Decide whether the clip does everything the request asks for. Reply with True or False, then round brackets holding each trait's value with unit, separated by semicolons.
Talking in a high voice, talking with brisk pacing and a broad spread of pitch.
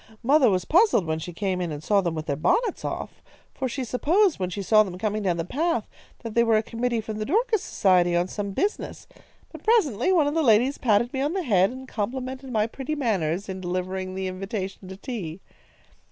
True (215 Hz; 220 wpm; 6.1 semitones)